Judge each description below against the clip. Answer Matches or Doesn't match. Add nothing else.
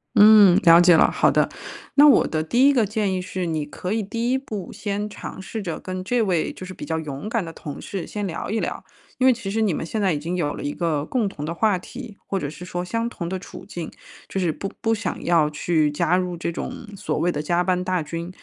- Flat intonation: Doesn't match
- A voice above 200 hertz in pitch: Doesn't match